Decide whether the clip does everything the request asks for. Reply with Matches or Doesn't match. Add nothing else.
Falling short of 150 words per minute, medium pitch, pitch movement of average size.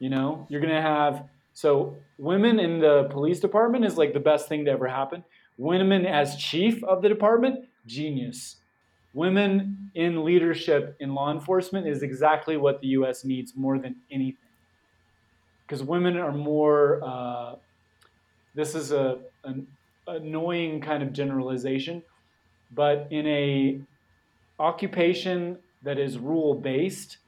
Matches